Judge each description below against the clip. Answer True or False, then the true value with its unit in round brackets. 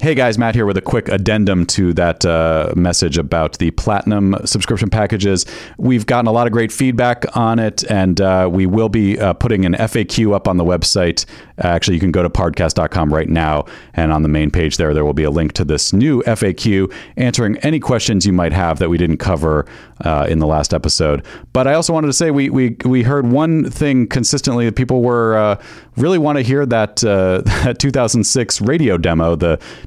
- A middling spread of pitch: False (5.7 semitones)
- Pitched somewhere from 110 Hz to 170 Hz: False (100 Hz)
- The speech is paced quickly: True (210 wpm)